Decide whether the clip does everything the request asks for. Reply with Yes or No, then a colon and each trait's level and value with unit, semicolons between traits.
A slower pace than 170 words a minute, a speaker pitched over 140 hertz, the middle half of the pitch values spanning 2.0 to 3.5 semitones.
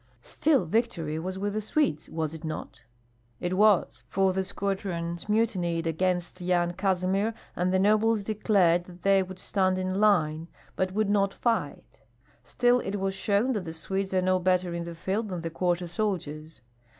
No: average, 175 wpm; medium, 185 Hz; average, 2.9 semitones